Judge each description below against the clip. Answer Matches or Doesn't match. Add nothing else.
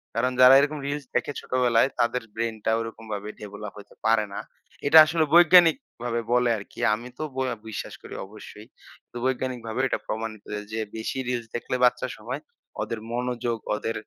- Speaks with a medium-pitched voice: Doesn't match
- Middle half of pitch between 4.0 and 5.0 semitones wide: Doesn't match